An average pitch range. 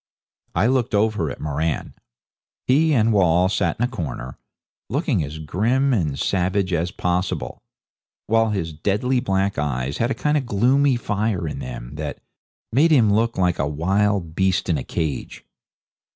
No: wide, 6.3 semitones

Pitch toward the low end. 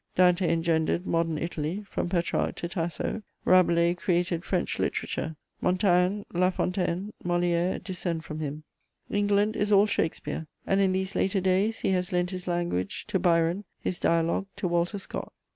No: medium, 180 Hz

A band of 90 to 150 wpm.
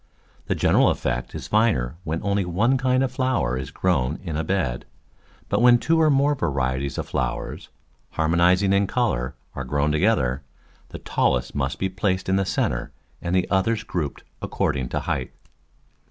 No: average, 170 wpm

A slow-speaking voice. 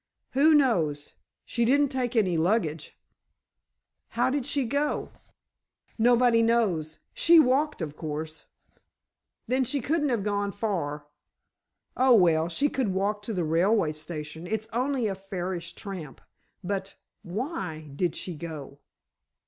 Yes: slow, 130 wpm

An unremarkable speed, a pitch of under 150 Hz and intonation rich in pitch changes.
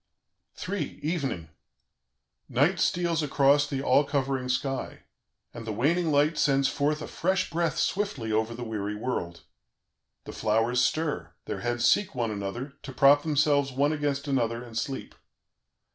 No: average, 145 wpm; low, 135 Hz; average, 4.2 semitones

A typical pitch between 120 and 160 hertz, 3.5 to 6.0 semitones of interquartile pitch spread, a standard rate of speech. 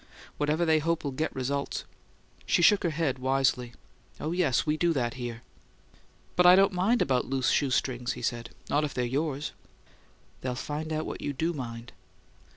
Yes: medium, 140 Hz; average, 4.1 semitones; average, 175 wpm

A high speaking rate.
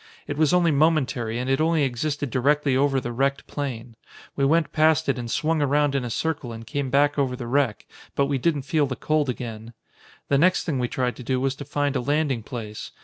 Yes: fast, 225 wpm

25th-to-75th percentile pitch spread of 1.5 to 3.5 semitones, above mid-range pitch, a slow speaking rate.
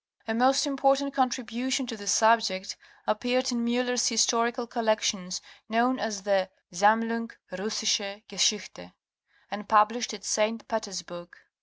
Yes: average, 3.2 semitones; high, 225 Hz; slow, 125 wpm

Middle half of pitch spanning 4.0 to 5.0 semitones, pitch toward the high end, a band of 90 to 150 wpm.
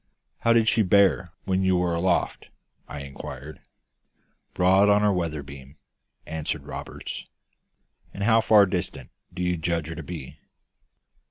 No: average, 4.3 semitones; very low, 90 Hz; average, 145 wpm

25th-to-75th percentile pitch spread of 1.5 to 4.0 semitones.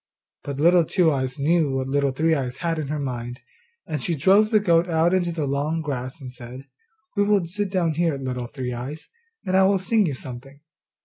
No: average, 4.7 semitones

